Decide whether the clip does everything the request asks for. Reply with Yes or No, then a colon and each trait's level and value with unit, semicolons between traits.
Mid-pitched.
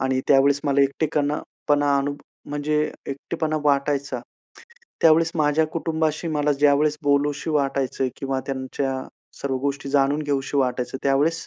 Yes: medium, 145 Hz